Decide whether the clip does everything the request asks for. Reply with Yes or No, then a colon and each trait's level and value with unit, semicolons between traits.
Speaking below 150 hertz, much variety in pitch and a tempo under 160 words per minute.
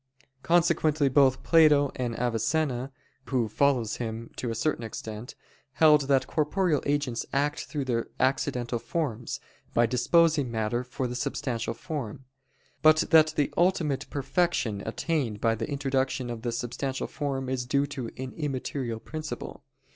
No: low, 135 Hz; average, 3.8 semitones; average, 140 wpm